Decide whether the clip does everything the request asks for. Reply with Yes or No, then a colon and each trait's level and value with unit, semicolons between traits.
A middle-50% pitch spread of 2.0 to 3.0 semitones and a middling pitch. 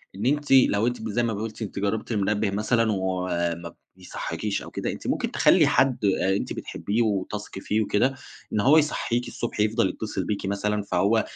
No: average, 2.7 semitones; low, 105 Hz